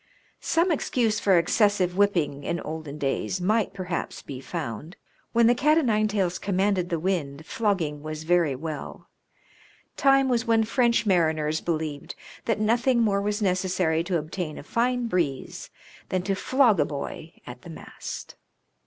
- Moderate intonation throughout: No, wide, 5.7 semitones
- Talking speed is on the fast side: No, average, 160 wpm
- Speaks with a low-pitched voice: No, medium, 185 Hz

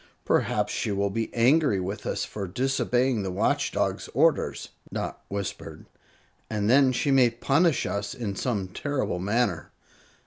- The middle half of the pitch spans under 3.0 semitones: No, average, 4.8 semitones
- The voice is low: Yes, low, 115 Hz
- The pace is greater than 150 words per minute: No, average, 145 wpm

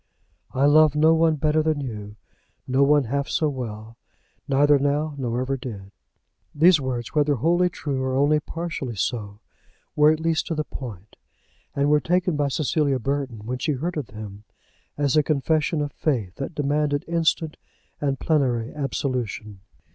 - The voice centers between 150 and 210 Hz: No, medium, 140 Hz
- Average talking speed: Yes, average, 160 wpm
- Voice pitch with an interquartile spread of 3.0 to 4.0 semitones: Yes, average, 3.3 semitones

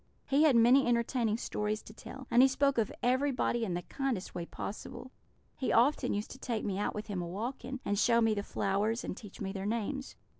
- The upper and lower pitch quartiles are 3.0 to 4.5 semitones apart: Yes, average, 4.1 semitones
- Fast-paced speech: Yes, fast, 220 wpm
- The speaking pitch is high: Yes, high, 230 Hz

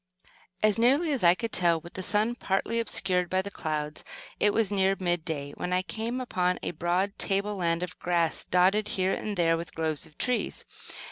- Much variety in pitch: No, average, 3.4 semitones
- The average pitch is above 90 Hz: Yes, medium, 185 Hz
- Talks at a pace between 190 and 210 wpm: Yes, average, 195 wpm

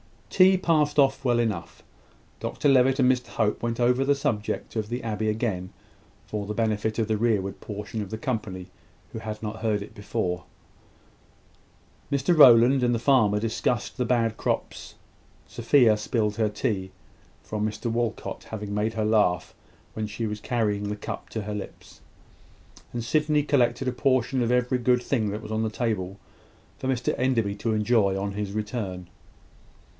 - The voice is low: Yes, low, 110 Hz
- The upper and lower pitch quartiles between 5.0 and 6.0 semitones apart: No, average, 3.0 semitones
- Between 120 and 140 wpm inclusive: No, average, 170 wpm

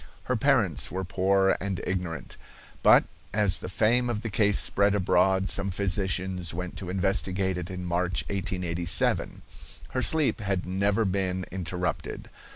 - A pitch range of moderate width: No, narrow, 1.8 semitones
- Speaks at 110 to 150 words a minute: Yes, average, 145 wpm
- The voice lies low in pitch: Yes, very low, 95 Hz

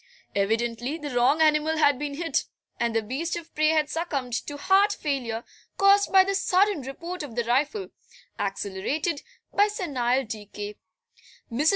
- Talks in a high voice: Yes, very high, 290 Hz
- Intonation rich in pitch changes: Yes, wide, 5.9 semitones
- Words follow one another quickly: No, average, 155 wpm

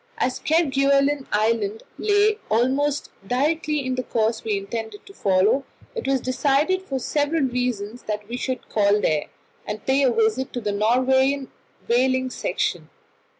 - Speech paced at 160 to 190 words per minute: No, average, 150 wpm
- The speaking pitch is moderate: No, very high, 255 Hz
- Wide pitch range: No, average, 4.0 semitones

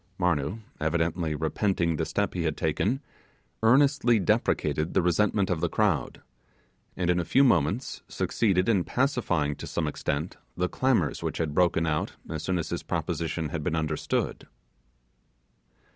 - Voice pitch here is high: No, very low, 85 Hz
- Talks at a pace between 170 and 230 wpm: No, average, 150 wpm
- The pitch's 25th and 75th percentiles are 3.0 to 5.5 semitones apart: Yes, average, 4.8 semitones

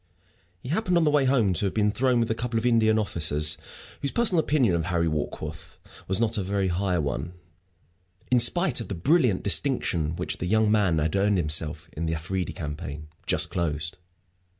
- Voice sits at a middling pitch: No, very low, 95 Hz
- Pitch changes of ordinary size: No, wide, 6.5 semitones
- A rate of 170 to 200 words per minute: Yes, average, 195 wpm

